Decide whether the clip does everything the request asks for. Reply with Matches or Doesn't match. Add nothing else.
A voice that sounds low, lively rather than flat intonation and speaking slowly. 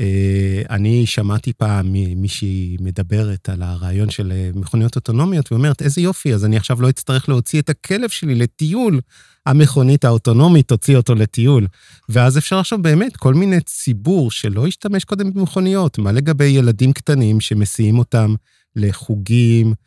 Doesn't match